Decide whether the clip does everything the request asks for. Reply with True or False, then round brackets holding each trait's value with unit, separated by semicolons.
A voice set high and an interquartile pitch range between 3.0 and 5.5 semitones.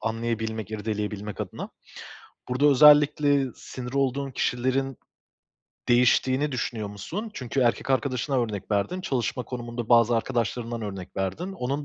False (125 Hz; 3.6 semitones)